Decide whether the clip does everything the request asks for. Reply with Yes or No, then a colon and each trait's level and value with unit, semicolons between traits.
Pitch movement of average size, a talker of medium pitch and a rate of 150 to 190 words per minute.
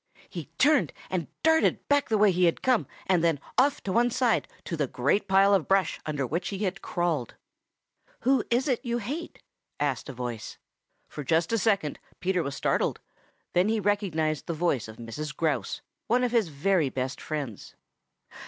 No: wide, 6.9 semitones; medium, 180 Hz; average, 180 wpm